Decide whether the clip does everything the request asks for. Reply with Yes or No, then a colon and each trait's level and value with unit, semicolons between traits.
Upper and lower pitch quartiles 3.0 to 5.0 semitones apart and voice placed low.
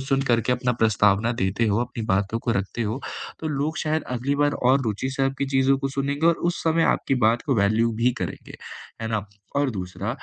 Yes: average, 3.8 semitones; low, 125 Hz